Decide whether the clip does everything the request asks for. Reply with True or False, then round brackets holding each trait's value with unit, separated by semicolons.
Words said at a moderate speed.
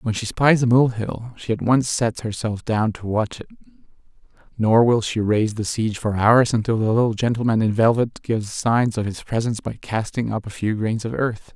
False (220 wpm)